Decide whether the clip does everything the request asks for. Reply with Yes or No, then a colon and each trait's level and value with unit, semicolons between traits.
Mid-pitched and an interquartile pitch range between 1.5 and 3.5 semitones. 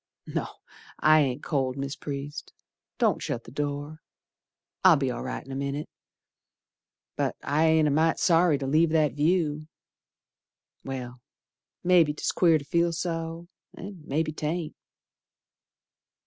Yes: medium, 150 Hz; average, 2.8 semitones